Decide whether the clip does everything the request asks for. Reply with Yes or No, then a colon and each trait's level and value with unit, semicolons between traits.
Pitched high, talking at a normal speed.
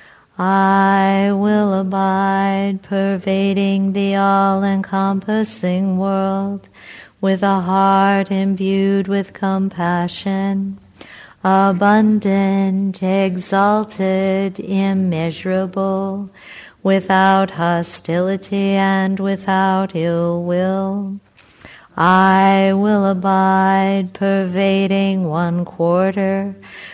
No: high, 195 Hz; slow, 65 wpm